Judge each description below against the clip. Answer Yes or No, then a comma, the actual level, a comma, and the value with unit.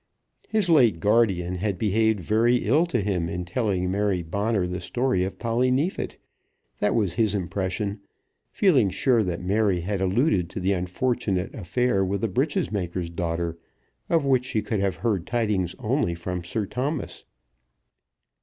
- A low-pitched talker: Yes, low, 100 Hz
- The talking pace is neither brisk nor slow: Yes, average, 155 wpm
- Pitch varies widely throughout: No, average, 4.7 semitones